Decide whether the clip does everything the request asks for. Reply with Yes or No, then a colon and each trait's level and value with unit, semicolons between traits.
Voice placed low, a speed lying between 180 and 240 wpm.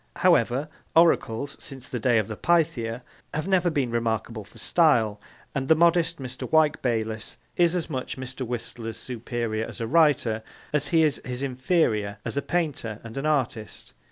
No: low, 130 Hz; average, 170 wpm